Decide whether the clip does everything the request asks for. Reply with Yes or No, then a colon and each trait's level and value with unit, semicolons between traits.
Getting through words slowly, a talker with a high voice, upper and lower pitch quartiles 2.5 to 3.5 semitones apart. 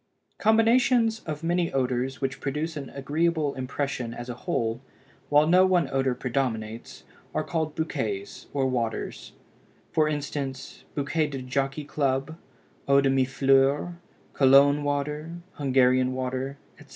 No: slow, 130 wpm; medium, 140 Hz; average, 2.8 semitones